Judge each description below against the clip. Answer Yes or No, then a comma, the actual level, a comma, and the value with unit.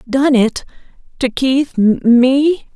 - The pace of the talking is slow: Yes, slow, 65 wpm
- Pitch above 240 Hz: Yes, very high, 260 Hz